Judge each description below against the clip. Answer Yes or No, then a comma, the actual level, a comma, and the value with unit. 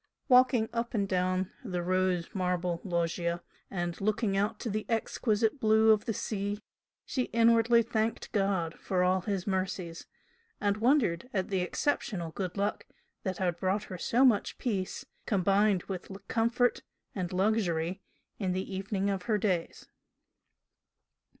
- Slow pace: No, average, 145 wpm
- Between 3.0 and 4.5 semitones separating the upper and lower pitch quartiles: Yes, average, 3.3 semitones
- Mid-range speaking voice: No, high, 195 Hz